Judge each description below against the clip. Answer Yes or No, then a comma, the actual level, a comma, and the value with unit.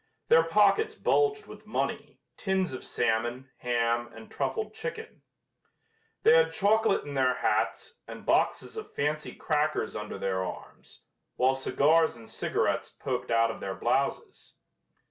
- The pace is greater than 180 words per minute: No, average, 140 wpm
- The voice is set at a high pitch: No, medium, 145 Hz